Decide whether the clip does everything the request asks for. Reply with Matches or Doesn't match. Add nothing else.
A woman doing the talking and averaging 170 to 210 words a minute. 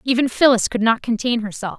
Matches